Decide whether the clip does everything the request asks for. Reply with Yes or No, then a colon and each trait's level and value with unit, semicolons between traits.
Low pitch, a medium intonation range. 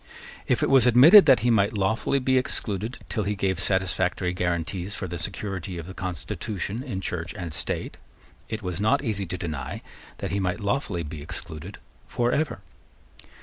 Yes: very low, 95 Hz; average, 4.0 semitones